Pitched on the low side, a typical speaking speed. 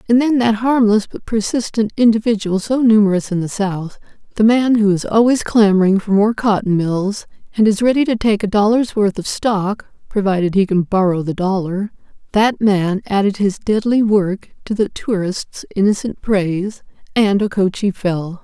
No: high, 205 Hz; average, 165 wpm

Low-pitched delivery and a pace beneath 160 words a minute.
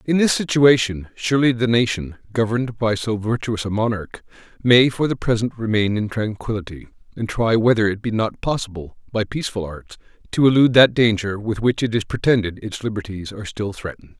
No: low, 110 Hz; average, 180 wpm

